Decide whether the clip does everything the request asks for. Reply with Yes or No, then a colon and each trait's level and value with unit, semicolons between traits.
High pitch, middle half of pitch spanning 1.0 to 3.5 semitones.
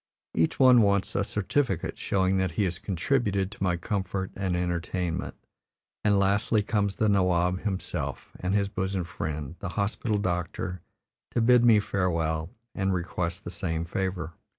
No: very low, 95 Hz; narrow, 2.5 semitones